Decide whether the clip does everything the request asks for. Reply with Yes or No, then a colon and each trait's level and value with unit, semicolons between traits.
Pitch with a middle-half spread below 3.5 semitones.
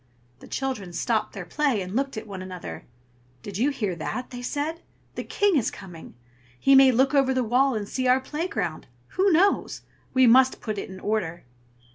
No: wide, 5.5 semitones